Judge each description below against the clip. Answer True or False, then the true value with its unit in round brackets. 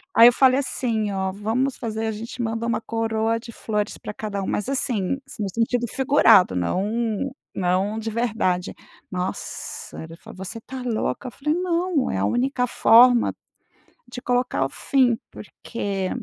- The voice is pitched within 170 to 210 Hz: False (225 Hz)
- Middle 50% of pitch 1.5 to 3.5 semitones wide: True (3.2 semitones)